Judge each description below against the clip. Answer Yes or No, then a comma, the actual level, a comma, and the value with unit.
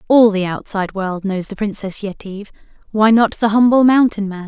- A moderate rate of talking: Yes, average, 175 wpm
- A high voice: Yes, high, 205 Hz